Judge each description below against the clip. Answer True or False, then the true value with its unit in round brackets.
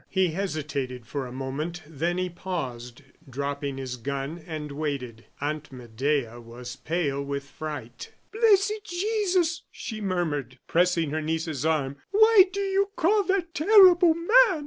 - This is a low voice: False (155 Hz)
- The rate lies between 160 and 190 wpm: False (140 wpm)